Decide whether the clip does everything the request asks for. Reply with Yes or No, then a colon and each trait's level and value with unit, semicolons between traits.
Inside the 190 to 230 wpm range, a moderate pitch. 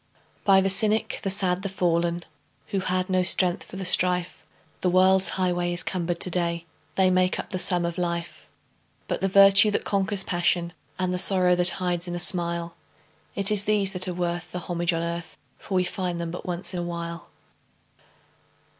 Yes: average, 195 wpm; medium, 180 Hz